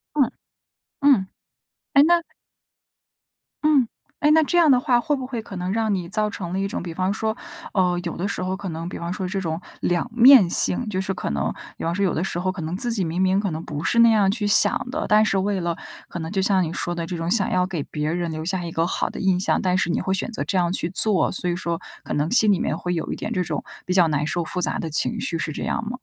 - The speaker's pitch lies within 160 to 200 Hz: Yes, medium, 185 Hz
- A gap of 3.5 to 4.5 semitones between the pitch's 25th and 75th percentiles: Yes, average, 3.8 semitones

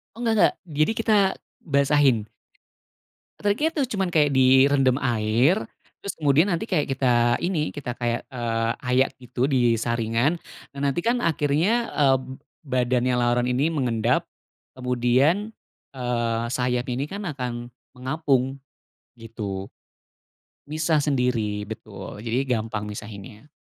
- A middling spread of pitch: Yes, average, 4.2 semitones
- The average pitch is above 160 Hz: No, low, 130 Hz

